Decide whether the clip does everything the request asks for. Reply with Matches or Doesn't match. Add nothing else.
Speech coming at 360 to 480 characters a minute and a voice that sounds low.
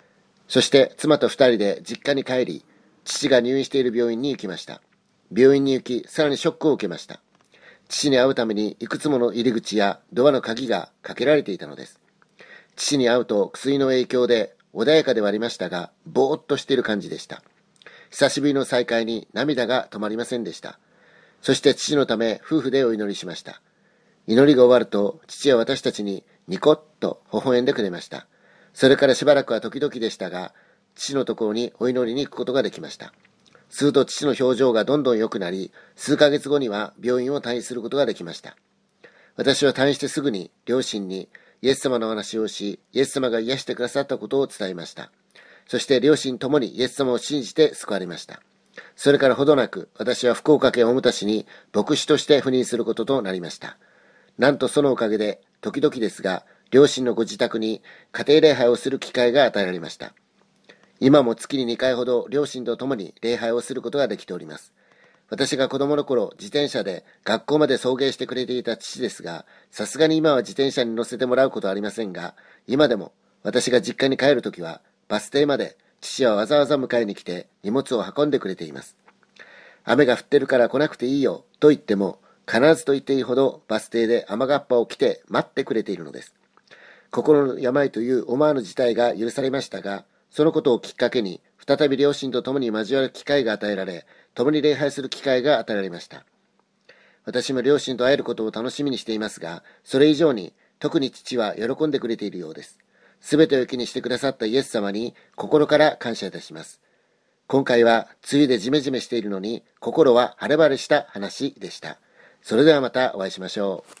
Matches